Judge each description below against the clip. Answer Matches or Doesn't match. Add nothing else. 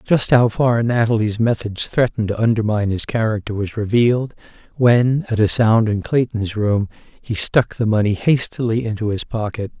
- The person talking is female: Doesn't match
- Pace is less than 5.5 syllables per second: Matches